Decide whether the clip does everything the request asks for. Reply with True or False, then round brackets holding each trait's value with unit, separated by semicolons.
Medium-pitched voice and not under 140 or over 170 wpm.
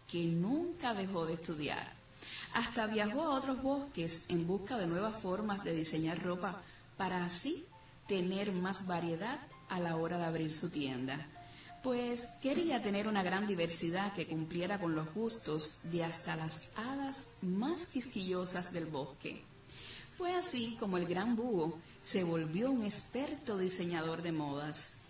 True (180 Hz; 150 wpm)